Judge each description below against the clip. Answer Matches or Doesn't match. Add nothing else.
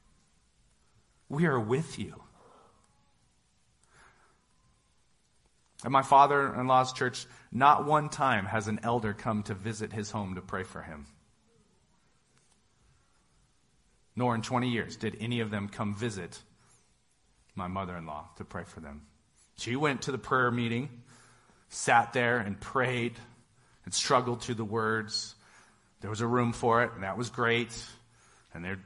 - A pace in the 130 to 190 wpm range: Matches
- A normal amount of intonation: Matches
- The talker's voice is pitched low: Matches